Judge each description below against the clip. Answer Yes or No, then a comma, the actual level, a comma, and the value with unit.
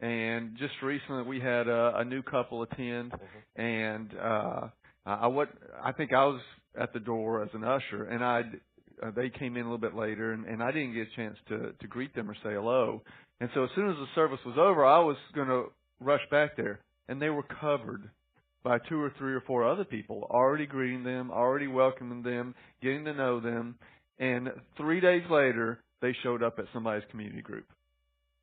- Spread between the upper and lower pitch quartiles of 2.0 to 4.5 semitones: Yes, average, 2.8 semitones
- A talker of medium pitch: No, low, 125 Hz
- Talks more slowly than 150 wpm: No, fast, 205 wpm